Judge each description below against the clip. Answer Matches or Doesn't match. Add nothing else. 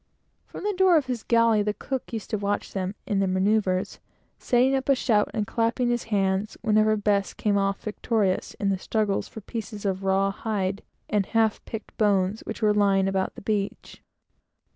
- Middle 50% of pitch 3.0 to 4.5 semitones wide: Doesn't match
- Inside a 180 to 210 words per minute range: Matches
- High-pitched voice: Matches